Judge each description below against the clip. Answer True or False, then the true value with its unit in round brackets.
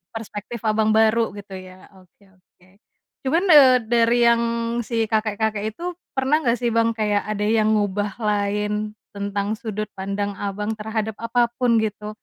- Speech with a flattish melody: True (2.1 semitones)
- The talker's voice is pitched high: True (215 Hz)